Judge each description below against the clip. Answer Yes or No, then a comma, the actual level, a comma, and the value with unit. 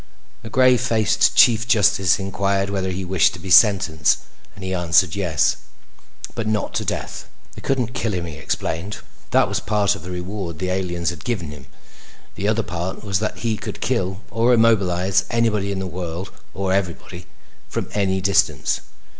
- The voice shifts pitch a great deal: No, average, 3.2 semitones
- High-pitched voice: No, very low, 95 Hz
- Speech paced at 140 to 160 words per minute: No, average, 175 wpm